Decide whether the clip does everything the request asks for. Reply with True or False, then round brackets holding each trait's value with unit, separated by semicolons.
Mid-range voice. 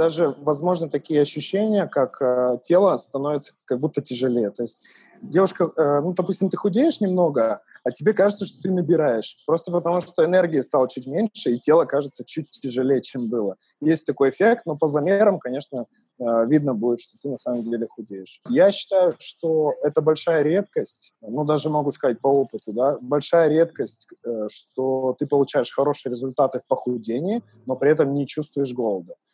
True (150 Hz)